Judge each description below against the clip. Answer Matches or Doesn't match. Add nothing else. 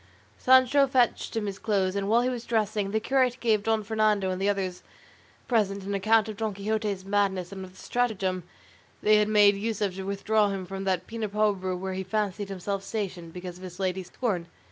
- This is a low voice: Doesn't match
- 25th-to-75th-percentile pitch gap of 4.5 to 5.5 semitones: Doesn't match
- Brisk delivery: Matches